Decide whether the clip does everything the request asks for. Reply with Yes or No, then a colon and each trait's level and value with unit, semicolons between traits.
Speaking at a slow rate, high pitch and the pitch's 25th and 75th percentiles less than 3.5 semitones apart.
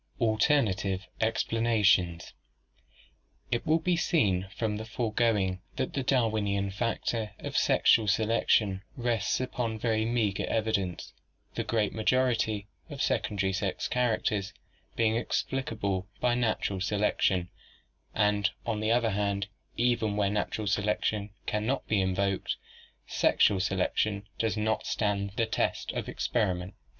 No: slow, 125 wpm; low, 105 Hz; narrow, 2.6 semitones